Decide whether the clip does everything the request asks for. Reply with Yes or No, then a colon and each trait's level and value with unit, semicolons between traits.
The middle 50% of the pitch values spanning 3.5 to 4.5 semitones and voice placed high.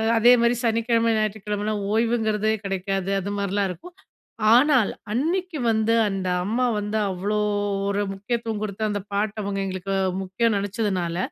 No: narrow, 2.6 semitones; high, 210 Hz